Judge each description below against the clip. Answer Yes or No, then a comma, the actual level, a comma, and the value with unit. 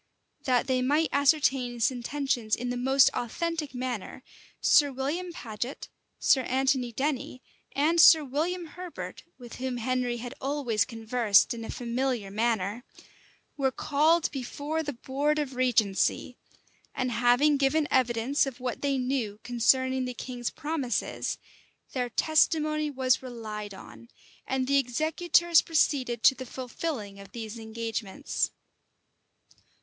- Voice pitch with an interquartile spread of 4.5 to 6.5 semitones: No, average, 3.2 semitones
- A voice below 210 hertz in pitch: No, very high, 255 Hz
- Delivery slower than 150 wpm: Yes, slow, 135 wpm